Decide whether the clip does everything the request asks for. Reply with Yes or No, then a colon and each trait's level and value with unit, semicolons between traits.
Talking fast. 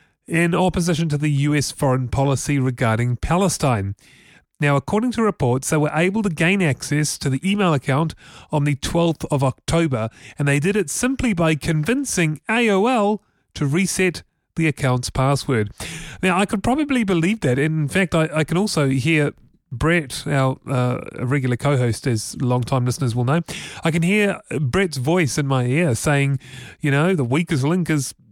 No: average, 170 wpm